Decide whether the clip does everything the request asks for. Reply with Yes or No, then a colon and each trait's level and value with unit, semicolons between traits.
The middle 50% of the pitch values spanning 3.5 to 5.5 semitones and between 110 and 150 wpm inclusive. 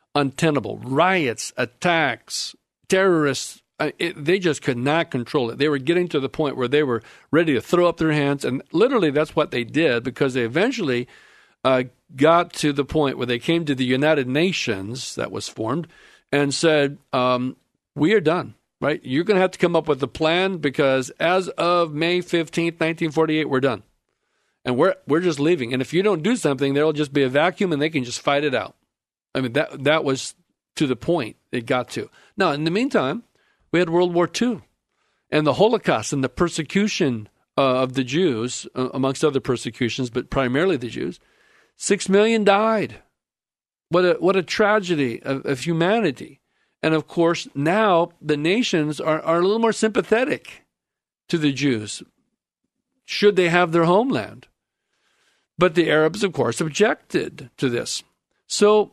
No: average, 4.7 semitones; average, 180 wpm